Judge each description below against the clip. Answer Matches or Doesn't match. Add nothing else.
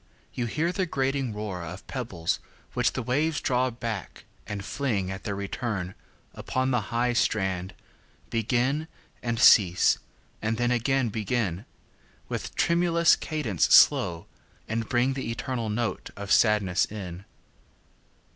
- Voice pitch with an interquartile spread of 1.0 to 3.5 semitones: Doesn't match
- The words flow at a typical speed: Doesn't match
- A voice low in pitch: Matches